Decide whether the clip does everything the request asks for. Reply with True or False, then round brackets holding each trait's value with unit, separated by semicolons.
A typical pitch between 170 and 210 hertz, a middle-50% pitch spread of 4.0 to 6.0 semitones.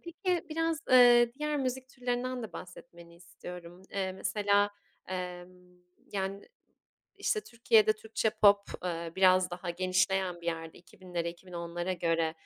True (190 Hz; 5.4 semitones)